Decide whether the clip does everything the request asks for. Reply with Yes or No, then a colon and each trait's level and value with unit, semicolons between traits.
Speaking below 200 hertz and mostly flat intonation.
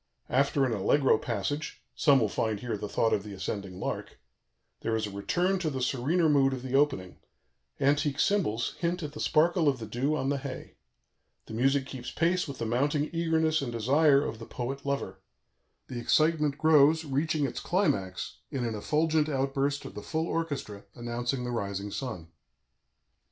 No: low, 135 Hz; average, 4.8 semitones